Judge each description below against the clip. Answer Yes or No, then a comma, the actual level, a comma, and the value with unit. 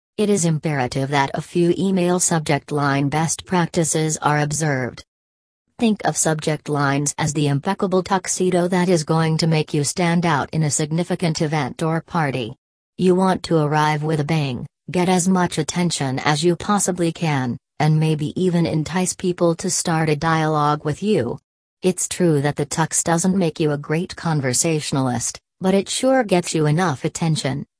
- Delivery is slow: No, average, 170 wpm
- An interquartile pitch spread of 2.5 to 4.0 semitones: Yes, average, 3.1 semitones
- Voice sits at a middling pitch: Yes, medium, 160 Hz